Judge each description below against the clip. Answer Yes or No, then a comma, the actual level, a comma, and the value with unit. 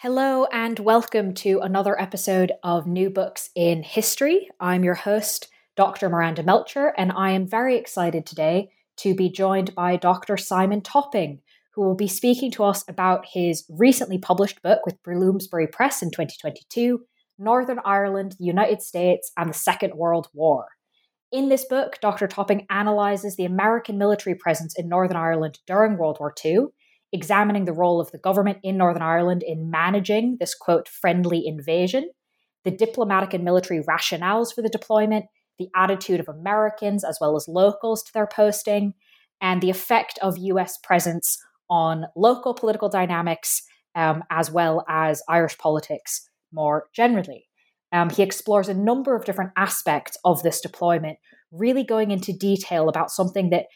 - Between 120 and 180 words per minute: Yes, average, 160 wpm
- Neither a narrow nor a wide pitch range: Yes, average, 3.6 semitones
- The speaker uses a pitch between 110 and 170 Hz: No, high, 190 Hz